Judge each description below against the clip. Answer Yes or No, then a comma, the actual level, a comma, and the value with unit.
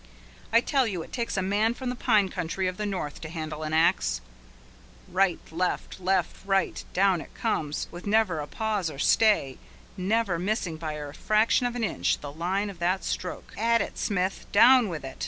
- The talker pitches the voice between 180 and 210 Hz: Yes, high, 190 Hz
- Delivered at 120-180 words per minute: No, average, 195 wpm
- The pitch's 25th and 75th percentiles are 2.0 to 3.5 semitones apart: No, average, 4.9 semitones